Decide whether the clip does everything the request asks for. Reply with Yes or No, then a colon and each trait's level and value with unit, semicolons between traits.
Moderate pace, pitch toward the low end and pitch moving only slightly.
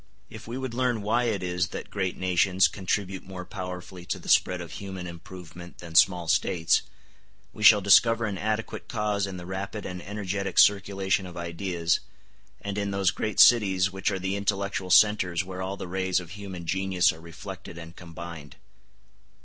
Yes: average, 175 wpm; very low, 95 Hz; narrow, 2.1 semitones